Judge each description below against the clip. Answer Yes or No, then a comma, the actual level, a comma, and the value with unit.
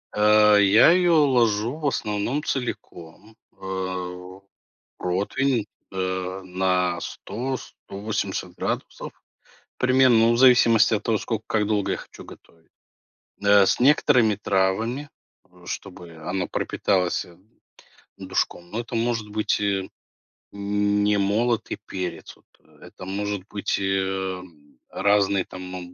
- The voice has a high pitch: No, low, 105 Hz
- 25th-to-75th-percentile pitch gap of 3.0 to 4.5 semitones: Yes, average, 3.4 semitones